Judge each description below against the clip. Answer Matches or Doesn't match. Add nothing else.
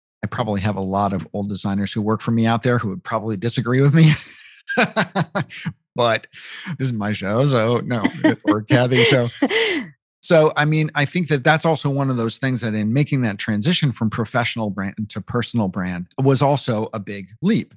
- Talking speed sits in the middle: Matches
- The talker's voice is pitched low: Matches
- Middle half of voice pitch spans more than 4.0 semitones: Matches